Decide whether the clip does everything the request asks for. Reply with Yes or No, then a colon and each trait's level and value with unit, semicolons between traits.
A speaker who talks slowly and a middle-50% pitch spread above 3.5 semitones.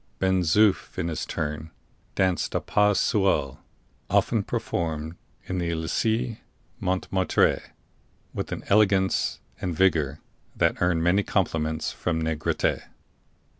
No: slow, 115 wpm; average, 3.1 semitones